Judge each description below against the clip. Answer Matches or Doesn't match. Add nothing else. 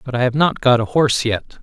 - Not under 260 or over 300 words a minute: Matches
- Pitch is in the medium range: Doesn't match